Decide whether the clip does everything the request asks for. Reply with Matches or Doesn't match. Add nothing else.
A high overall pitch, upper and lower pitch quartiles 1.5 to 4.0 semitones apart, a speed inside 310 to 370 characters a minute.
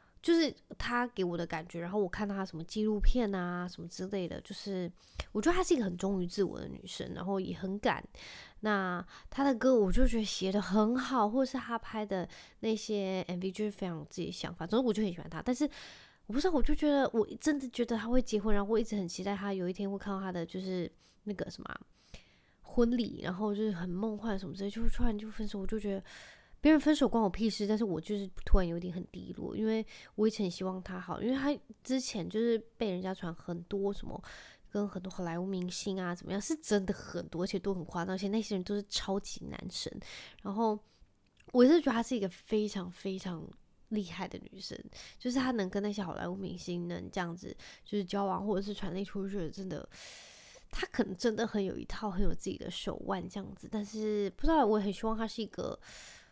Matches